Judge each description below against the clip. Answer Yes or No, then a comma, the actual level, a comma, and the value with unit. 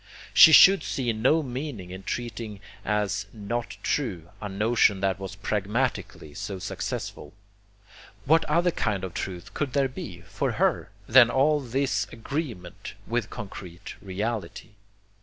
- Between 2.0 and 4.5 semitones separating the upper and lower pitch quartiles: No, average, 5.3 semitones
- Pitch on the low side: Yes, low, 110 Hz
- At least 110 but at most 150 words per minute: Yes, slow, 135 wpm